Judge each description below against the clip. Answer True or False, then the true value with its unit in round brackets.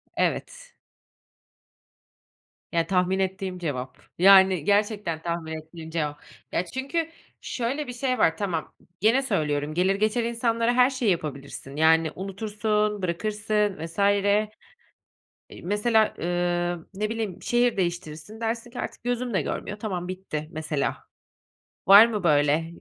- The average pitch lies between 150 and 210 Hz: True (190 Hz)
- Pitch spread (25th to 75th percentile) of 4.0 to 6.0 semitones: True (5.3 semitones)